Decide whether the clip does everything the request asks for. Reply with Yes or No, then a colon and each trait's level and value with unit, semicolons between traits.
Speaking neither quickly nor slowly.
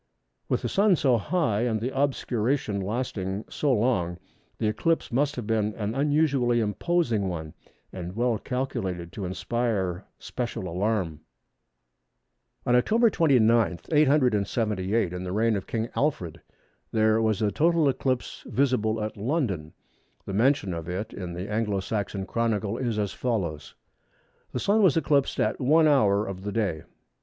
Yes: average, 145 wpm